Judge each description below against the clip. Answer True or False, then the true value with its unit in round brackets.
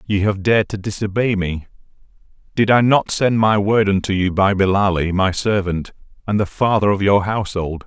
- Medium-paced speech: True (185 wpm)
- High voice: False (100 Hz)